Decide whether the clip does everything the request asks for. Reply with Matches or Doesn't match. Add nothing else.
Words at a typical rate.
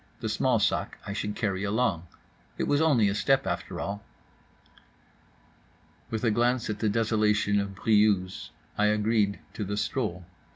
Matches